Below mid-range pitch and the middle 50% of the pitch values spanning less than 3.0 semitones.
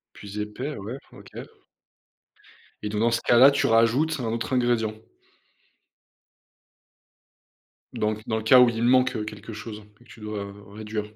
Yes: low, 115 Hz; narrow, 2.5 semitones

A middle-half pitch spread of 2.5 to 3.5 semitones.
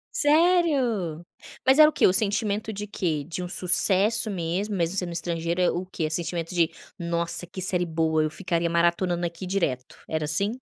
Yes: average, 3.2 semitones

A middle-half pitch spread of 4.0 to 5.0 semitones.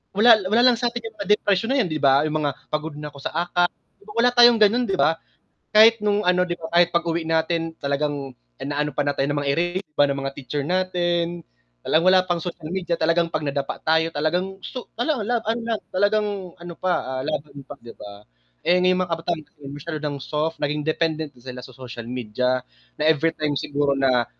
Yes: average, 4.3 semitones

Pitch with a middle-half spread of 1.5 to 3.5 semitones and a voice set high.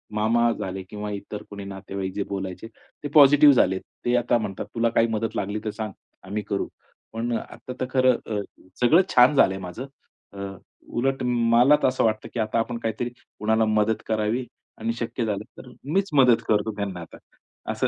No: average, 3.0 semitones; low, 110 Hz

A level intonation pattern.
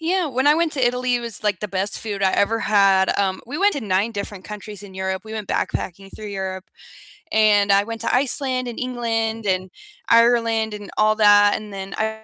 No: average, 3.2 semitones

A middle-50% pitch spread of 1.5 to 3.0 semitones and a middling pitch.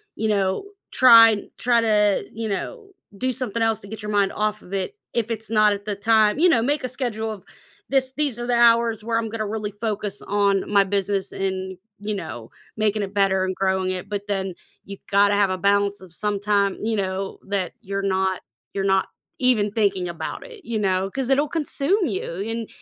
No: narrow, 2.6 semitones; high, 210 Hz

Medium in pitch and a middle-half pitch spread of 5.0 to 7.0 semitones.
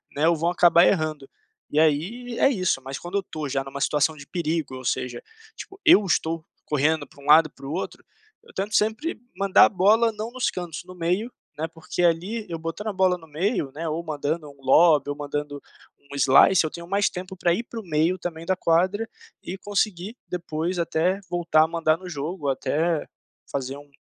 No: medium, 165 Hz; average, 3.9 semitones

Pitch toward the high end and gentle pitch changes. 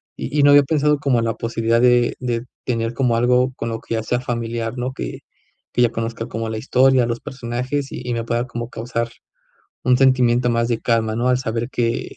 No: low, 120 Hz; narrow, 1.7 semitones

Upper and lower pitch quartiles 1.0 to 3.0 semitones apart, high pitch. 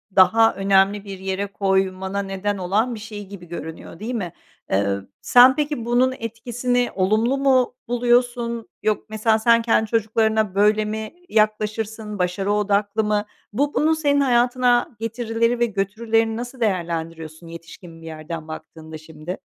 No: average, 3.6 semitones; high, 215 Hz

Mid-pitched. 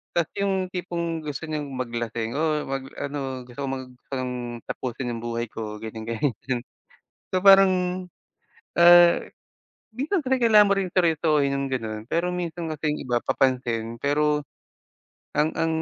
Yes: medium, 145 Hz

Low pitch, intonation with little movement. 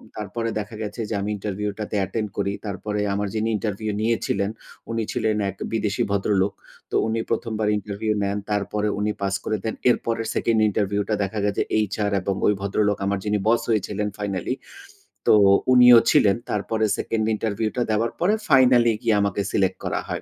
Yes: low, 105 Hz; narrow, 1.8 semitones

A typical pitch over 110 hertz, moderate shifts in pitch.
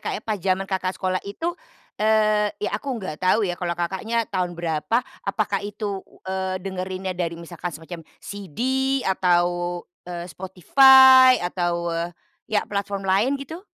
Yes: high, 190 Hz; average, 3.3 semitones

